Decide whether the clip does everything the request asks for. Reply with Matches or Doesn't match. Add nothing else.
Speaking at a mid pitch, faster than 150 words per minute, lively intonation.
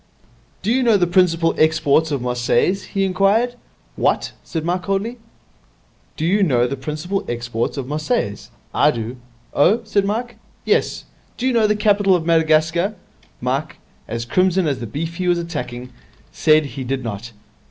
Matches